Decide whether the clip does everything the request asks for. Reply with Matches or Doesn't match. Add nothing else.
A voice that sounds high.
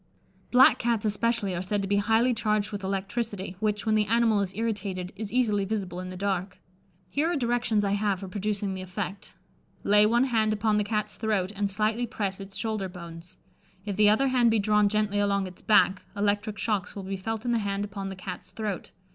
Matches